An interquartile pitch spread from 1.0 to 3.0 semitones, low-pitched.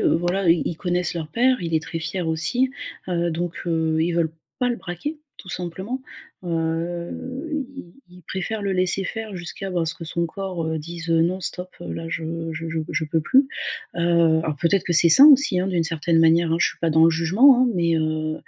No: average, 2.7 semitones; medium, 170 Hz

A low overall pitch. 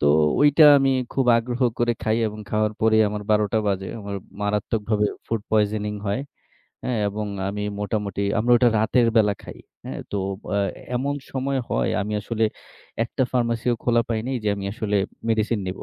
Yes: low, 110 Hz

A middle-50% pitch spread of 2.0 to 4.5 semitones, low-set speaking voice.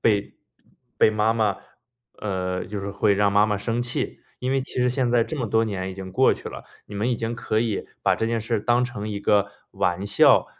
Yes: average, 2.8 semitones; low, 110 Hz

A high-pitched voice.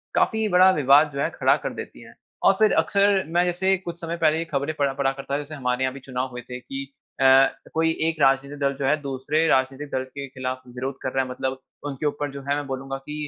No: medium, 140 Hz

